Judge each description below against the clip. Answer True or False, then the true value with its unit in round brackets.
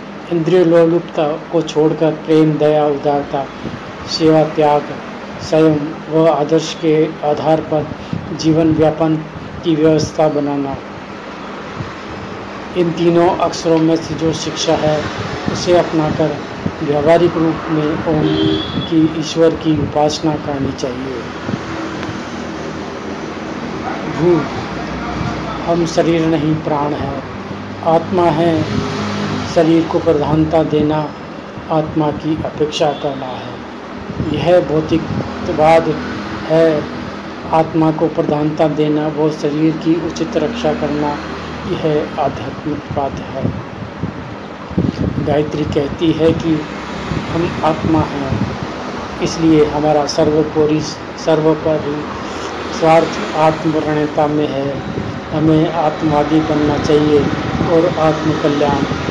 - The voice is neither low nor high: True (155 Hz)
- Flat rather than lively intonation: True (1.5 semitones)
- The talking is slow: True (95 wpm)